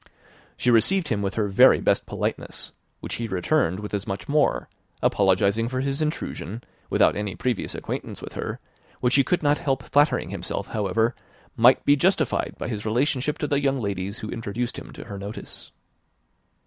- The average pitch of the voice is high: No, low, 115 Hz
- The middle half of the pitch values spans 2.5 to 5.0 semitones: No, wide, 5.4 semitones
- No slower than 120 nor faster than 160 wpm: No, average, 175 wpm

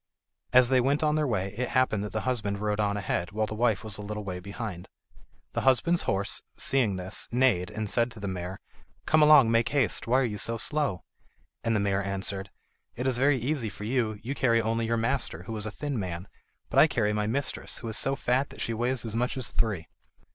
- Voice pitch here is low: Yes, low, 115 Hz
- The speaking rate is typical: No, fast, 230 wpm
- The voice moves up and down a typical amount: Yes, average, 3.9 semitones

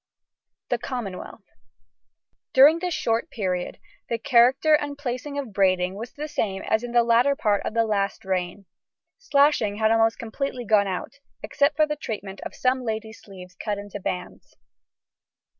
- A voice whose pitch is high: Yes, high, 225 Hz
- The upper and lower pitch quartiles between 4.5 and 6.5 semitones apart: Yes, average, 5.1 semitones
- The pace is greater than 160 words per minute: No, average, 155 wpm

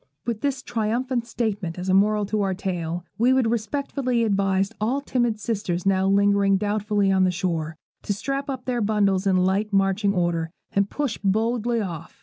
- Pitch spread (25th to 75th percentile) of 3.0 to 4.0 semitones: Yes, average, 3.5 semitones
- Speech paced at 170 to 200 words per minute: Yes, average, 175 wpm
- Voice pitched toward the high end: Yes, high, 205 Hz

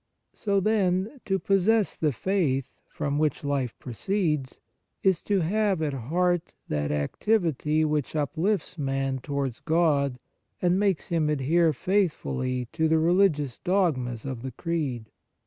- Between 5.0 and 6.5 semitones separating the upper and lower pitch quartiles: Yes, wide, 5.5 semitones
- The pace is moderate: No, slow, 130 wpm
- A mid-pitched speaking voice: Yes, medium, 155 Hz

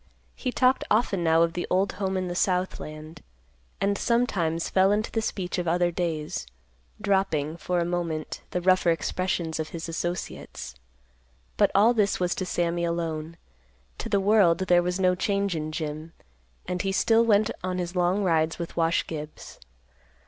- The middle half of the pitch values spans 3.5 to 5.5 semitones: No, average, 2.8 semitones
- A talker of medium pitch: Yes, medium, 175 Hz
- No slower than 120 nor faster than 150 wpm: No, average, 170 wpm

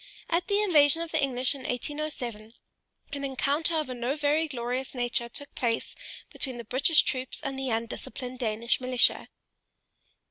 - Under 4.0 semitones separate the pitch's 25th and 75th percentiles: Yes, average, 3.4 semitones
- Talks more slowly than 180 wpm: Yes, average, 155 wpm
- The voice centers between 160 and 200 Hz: No, very high, 260 Hz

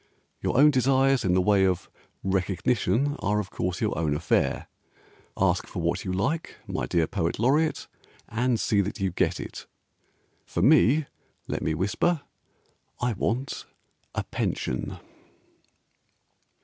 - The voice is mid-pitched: No, low, 100 Hz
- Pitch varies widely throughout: Yes, wide, 6.4 semitones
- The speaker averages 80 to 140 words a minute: Yes, slow, 135 wpm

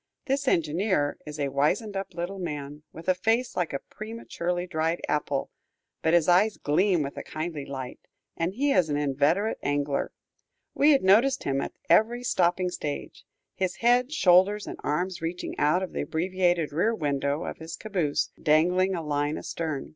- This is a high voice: No, medium, 175 Hz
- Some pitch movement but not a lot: Yes, average, 4.6 semitones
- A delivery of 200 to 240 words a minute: No, average, 170 wpm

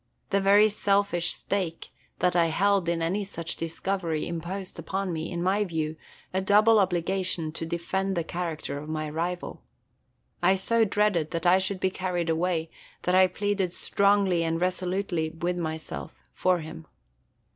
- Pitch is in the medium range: Yes, medium, 180 Hz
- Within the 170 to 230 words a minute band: No, average, 155 wpm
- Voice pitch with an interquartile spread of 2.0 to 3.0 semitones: Yes, average, 2.7 semitones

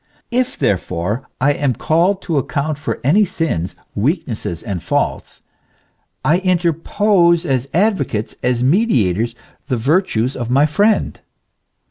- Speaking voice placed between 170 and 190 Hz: No, medium, 145 Hz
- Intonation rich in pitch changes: Yes, wide, 7.0 semitones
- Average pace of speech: No, slow, 120 wpm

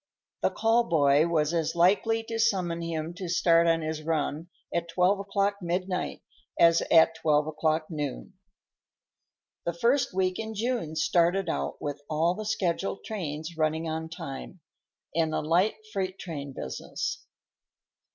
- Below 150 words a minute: Yes, average, 140 wpm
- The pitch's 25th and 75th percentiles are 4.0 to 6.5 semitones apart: No, average, 3.4 semitones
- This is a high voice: No, medium, 170 Hz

